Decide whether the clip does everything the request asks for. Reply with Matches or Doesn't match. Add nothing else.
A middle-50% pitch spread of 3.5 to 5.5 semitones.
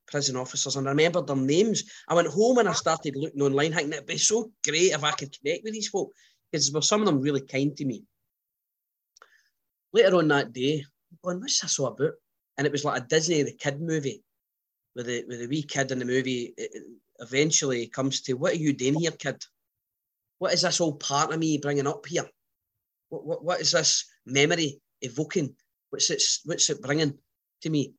Matches